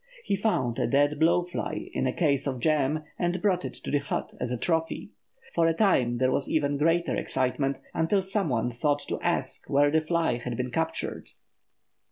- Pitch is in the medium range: Yes, medium, 150 Hz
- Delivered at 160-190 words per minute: No, average, 200 wpm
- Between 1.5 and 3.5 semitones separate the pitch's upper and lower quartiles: No, average, 4.4 semitones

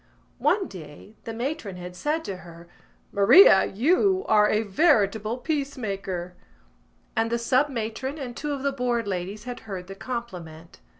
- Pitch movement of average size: No, wide, 6.0 semitones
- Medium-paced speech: Yes, average, 160 wpm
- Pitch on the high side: Yes, high, 225 Hz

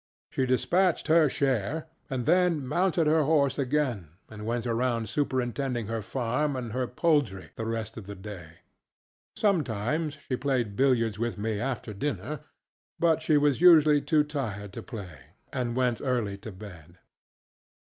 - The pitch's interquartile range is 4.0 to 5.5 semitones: Yes, average, 5.2 semitones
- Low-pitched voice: Yes, low, 125 Hz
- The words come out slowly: No, average, 150 wpm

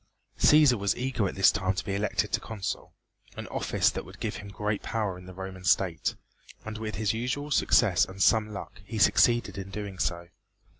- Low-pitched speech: Yes, low, 100 Hz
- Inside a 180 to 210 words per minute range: Yes, average, 195 wpm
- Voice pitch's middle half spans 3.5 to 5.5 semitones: No, average, 2.7 semitones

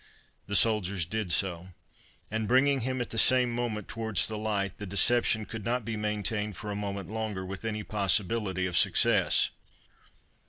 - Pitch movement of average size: No, narrow, 2.3 semitones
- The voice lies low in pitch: Yes, low, 105 Hz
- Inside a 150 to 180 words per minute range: Yes, average, 165 wpm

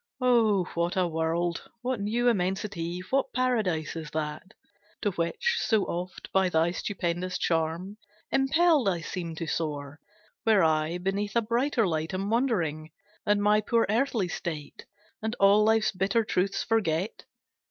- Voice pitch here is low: No, high, 190 Hz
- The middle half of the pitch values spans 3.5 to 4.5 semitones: No, average, 4.9 semitones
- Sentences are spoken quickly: No, average, 145 wpm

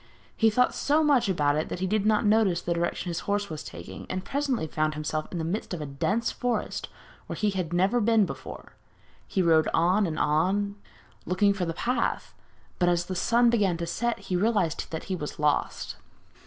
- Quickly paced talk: Yes, fast, 210 wpm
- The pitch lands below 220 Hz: Yes, medium, 185 Hz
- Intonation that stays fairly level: No, average, 4.6 semitones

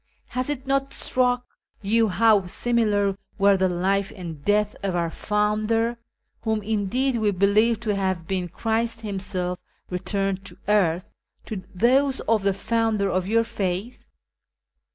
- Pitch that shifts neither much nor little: Yes, average, 3.2 semitones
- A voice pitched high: Yes, high, 210 Hz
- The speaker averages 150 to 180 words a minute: No, average, 140 wpm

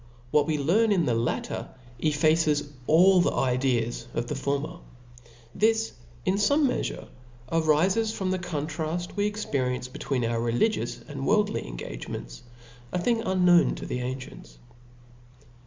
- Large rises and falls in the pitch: Yes, wide, 6.8 semitones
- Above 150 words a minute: No, average, 140 wpm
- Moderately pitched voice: Yes, medium, 155 Hz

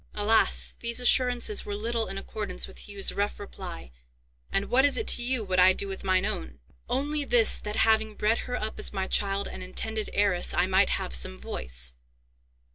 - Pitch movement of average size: Yes, average, 3.8 semitones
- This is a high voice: Yes, high, 205 Hz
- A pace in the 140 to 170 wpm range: No, average, 195 wpm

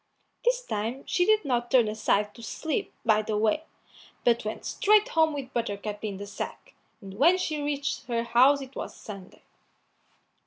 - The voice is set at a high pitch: Yes, high, 240 Hz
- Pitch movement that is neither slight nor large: No, wide, 5.9 semitones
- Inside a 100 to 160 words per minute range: No, average, 170 wpm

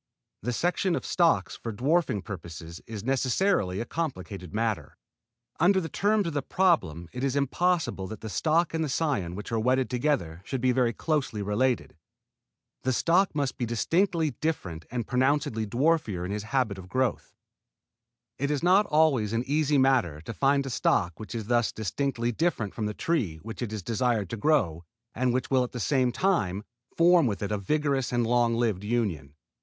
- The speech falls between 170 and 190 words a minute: Yes, average, 185 wpm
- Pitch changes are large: Yes, wide, 6.2 semitones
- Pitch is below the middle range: Yes, low, 125 Hz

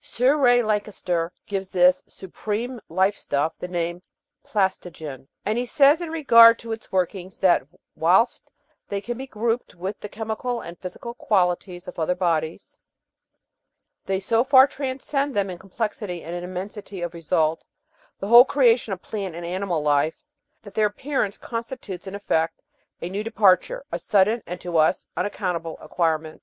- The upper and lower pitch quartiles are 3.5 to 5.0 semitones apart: Yes, average, 4.7 semitones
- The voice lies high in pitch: Yes, high, 195 Hz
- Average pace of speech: Yes, average, 165 wpm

